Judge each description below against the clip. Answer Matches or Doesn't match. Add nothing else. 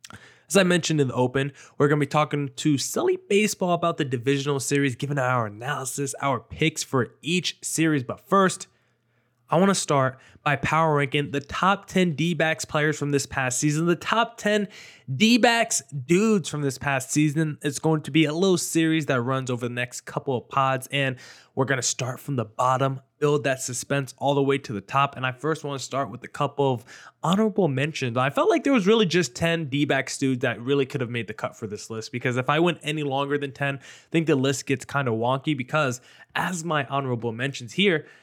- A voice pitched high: Doesn't match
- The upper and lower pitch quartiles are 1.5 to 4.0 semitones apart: Matches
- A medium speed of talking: Doesn't match